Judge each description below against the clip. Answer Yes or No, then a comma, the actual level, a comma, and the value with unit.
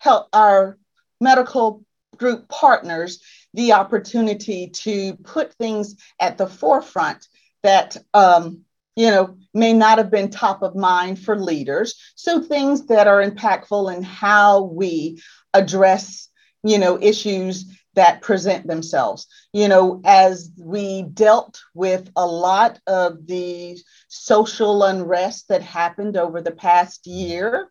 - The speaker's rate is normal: No, slow, 130 wpm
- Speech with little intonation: No, average, 3.0 semitones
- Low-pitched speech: No, high, 195 Hz